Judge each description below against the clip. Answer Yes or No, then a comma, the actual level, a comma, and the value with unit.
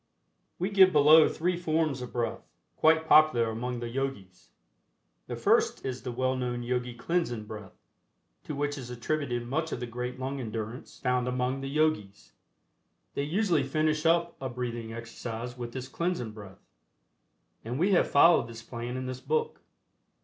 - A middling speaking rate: Yes, average, 165 wpm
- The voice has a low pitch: Yes, low, 130 Hz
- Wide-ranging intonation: No, average, 4.5 semitones